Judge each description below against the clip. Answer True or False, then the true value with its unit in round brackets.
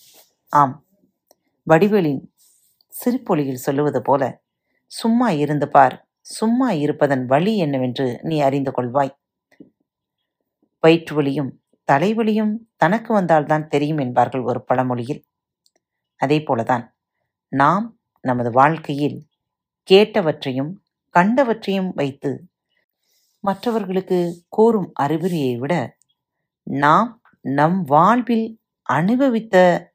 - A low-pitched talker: False (155 Hz)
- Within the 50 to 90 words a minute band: True (80 wpm)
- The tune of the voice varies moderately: False (6.6 semitones)